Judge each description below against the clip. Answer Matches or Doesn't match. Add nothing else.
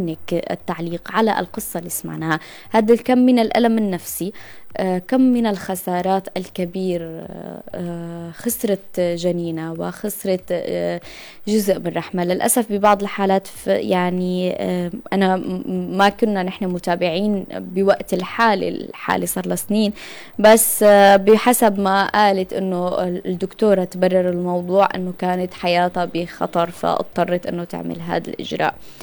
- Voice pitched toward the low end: Doesn't match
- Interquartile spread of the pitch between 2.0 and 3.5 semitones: Matches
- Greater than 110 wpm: Doesn't match